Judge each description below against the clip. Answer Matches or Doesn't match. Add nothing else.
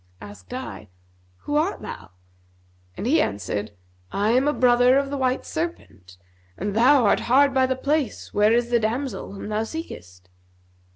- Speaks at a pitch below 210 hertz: Doesn't match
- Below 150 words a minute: Doesn't match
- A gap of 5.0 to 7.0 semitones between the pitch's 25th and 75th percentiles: Matches